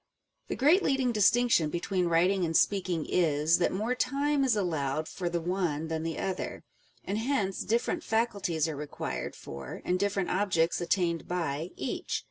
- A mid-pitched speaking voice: Yes, medium, 180 Hz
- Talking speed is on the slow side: No, average, 160 wpm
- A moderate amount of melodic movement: Yes, average, 4.5 semitones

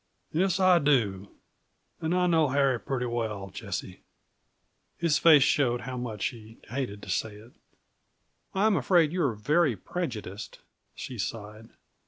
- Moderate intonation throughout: No, wide, 6.9 semitones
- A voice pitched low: Yes, low, 125 Hz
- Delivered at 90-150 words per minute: Yes, average, 140 wpm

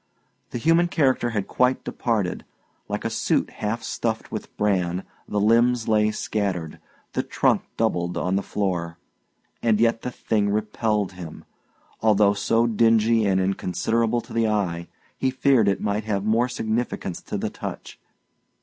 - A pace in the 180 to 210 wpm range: No, average, 150 wpm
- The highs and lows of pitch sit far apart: No, average, 2.8 semitones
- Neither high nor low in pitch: No, low, 110 Hz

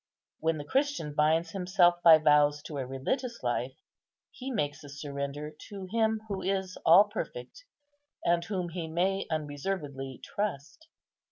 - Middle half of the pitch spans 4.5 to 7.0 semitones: Yes, average, 5.1 semitones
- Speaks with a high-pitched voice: No, medium, 165 Hz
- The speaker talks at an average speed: Yes, average, 145 wpm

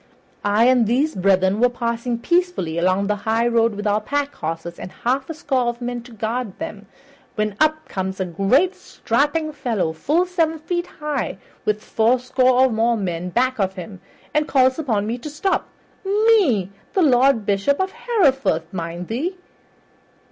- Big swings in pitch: Yes, wide, 6.1 semitones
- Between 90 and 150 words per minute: No, average, 165 wpm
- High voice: Yes, high, 240 Hz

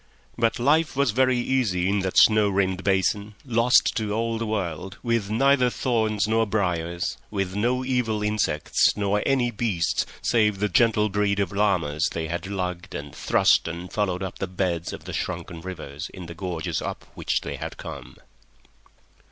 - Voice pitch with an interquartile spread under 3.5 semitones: No, average, 3.9 semitones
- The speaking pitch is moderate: No, low, 100 Hz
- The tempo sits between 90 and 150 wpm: No, average, 170 wpm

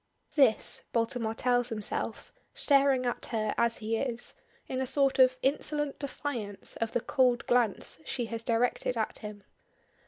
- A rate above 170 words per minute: No, average, 150 wpm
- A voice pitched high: Yes, high, 245 Hz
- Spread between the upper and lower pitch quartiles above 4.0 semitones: No, average, 2.7 semitones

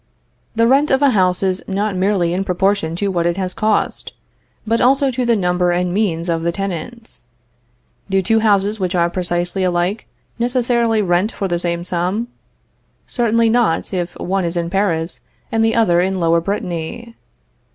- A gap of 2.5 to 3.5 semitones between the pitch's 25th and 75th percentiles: No, average, 4.2 semitones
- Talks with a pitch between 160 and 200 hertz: Yes, high, 190 Hz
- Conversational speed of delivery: Yes, average, 170 wpm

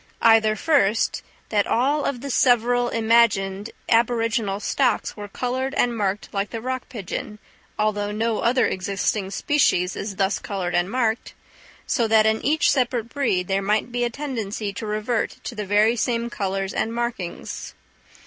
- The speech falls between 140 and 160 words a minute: Yes, average, 155 wpm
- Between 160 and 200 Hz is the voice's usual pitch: No, high, 220 Hz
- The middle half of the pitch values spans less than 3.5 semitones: Yes, average, 3.1 semitones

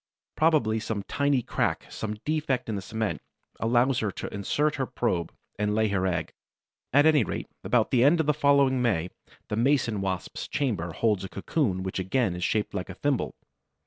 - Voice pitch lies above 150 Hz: No, low, 110 Hz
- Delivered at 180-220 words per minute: Yes, average, 185 wpm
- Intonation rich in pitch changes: Yes, wide, 6.1 semitones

